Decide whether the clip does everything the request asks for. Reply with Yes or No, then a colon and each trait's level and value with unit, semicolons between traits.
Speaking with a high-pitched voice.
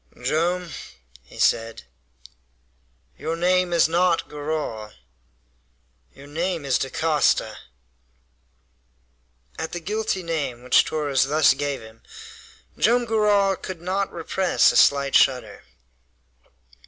No: medium, 160 Hz